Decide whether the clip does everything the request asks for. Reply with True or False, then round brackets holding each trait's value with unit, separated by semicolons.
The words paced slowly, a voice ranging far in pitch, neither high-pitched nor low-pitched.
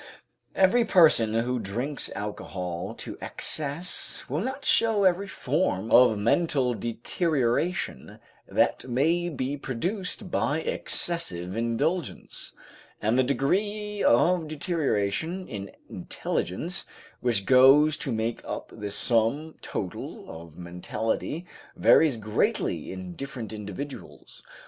False (105 wpm; 7.5 semitones; 130 Hz)